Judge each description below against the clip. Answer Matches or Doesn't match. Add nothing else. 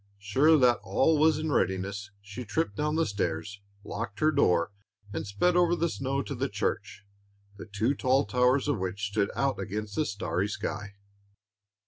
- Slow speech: Doesn't match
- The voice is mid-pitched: Doesn't match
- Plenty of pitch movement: Matches